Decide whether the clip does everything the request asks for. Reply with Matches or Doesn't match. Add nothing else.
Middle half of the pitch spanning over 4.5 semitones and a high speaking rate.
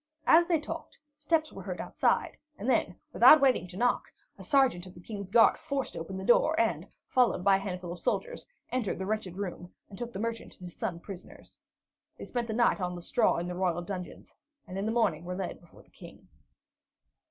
Matches